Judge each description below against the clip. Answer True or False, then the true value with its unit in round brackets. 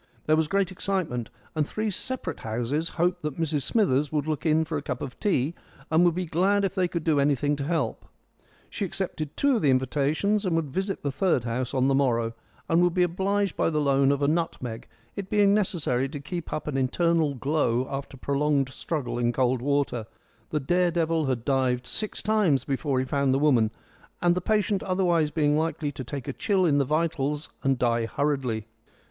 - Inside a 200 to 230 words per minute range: True (205 wpm)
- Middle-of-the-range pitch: True (150 Hz)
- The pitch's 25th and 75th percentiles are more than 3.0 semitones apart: True (4.6 semitones)